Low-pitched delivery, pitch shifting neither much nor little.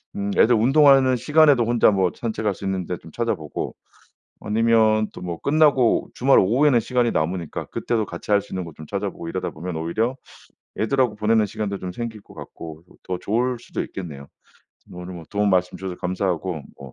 Yes: low, 105 Hz; average, 4.8 semitones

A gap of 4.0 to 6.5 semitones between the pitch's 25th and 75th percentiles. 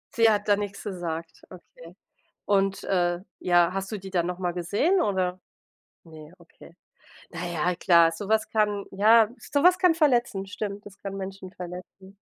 No: average, 2.8 semitones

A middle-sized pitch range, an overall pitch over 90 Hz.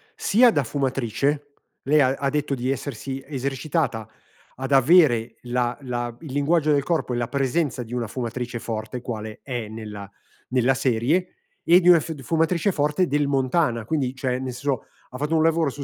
Yes: average, 3.6 semitones; low, 135 Hz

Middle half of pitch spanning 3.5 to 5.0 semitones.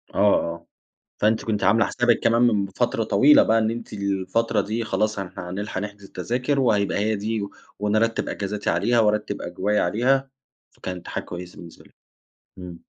No: narrow, 2.6 semitones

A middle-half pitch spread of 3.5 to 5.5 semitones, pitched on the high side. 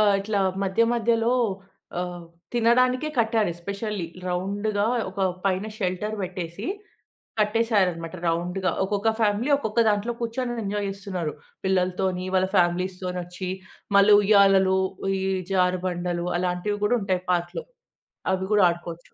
No: average, 2.8 semitones; high, 195 Hz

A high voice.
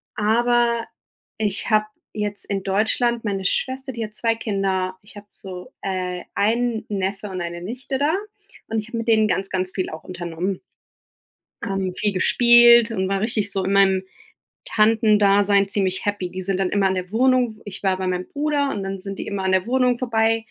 Yes: high, 205 Hz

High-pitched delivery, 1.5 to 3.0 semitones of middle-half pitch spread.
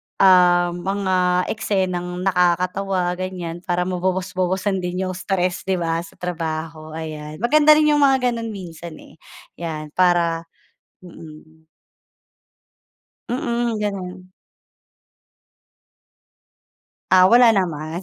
No: medium, 180 Hz; narrow, 2.4 semitones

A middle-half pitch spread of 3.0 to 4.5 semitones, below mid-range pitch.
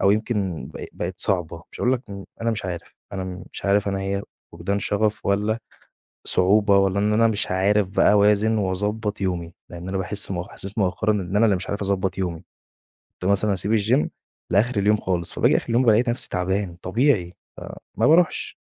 No: narrow, 2.4 semitones; low, 100 Hz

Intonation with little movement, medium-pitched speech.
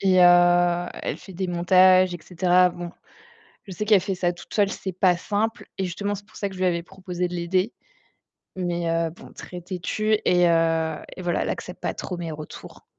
Yes: narrow, 1.5 semitones; medium, 180 Hz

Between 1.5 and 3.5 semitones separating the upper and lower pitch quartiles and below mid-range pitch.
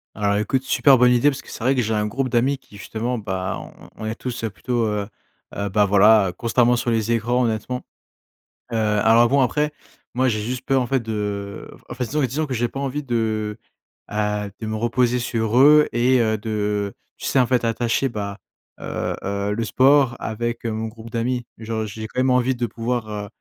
Yes: average, 2.8 semitones; low, 115 Hz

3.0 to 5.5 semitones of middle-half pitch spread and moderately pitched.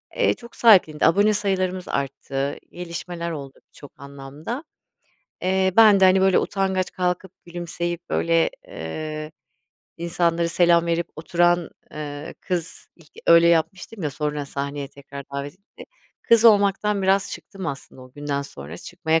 Yes: average, 4.4 semitones; medium, 170 Hz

